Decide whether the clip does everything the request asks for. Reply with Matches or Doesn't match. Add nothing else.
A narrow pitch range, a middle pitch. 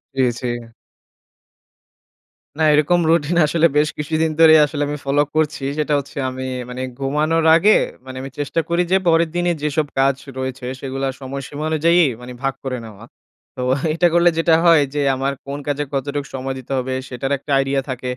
Doesn't match